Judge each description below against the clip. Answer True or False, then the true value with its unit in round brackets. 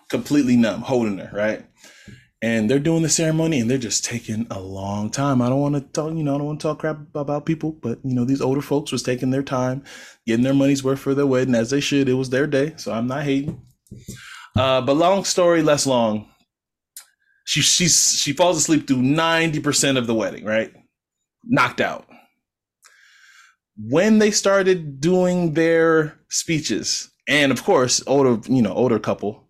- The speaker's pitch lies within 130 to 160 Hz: True (140 Hz)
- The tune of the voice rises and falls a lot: False (4.1 semitones)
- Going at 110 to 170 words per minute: False (190 wpm)